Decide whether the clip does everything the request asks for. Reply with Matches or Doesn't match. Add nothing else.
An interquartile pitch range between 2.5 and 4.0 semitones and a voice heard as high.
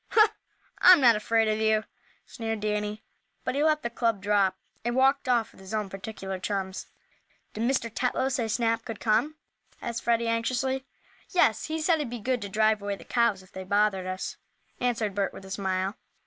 Matches